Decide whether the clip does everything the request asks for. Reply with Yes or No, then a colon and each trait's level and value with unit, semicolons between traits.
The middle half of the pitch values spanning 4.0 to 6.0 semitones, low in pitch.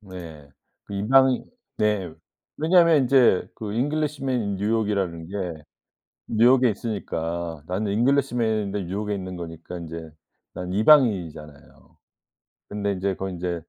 Yes: average, 5.3 semitones; low, 100 Hz